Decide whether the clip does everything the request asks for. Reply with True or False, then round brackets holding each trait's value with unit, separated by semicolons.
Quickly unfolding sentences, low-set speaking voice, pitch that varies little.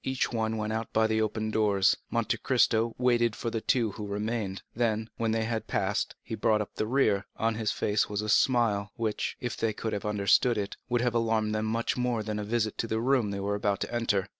True (240 wpm; 110 Hz; 1.7 semitones)